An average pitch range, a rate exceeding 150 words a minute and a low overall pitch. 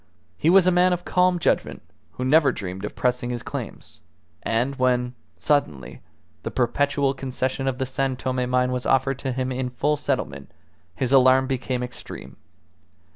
No: narrow, 1.9 semitones; average, 165 wpm; low, 130 Hz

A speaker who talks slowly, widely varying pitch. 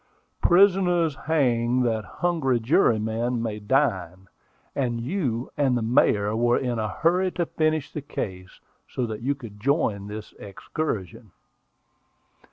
Yes: slow, 130 wpm; wide, 5.7 semitones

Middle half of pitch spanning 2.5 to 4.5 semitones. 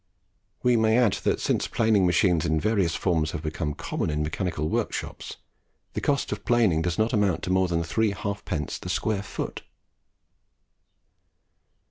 No: average, 5.1 semitones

